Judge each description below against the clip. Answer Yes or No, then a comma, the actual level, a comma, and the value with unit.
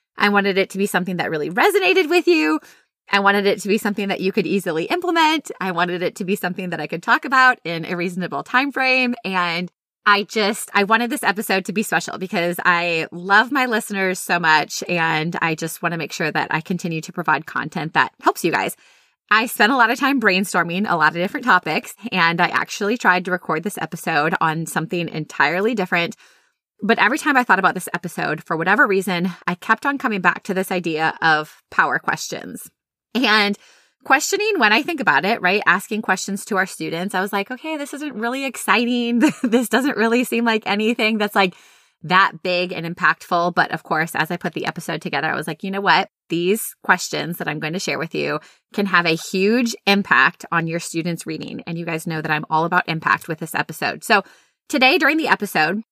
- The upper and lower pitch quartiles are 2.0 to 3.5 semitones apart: No, average, 4.7 semitones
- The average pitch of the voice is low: No, high, 190 Hz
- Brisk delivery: Yes, fast, 215 wpm